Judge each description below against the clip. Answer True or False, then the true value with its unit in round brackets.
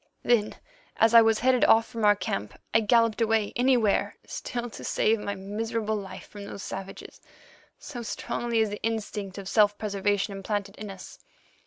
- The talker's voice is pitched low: False (215 Hz)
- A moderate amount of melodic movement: False (2.1 semitones)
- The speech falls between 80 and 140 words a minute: False (170 wpm)